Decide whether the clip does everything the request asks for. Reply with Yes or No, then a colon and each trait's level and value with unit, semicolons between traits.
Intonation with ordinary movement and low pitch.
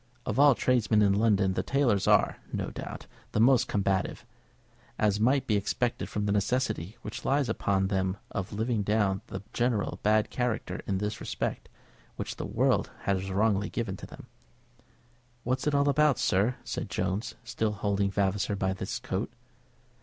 Yes: average, 3.5 semitones; low, 105 Hz